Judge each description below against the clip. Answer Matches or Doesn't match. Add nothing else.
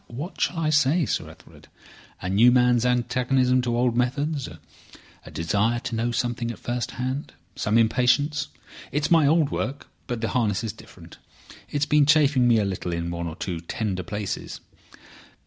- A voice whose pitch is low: Matches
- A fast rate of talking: Doesn't match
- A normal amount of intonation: Matches